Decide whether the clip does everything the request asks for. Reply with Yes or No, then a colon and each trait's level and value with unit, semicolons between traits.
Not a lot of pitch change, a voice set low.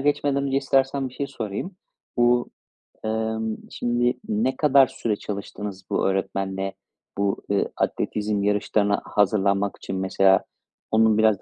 No: average, 4.0 semitones; low, 110 Hz